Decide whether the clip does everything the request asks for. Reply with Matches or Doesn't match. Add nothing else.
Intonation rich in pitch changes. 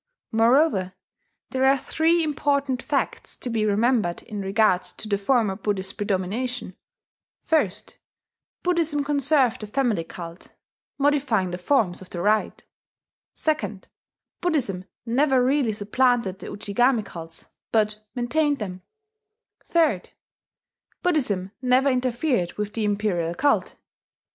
Matches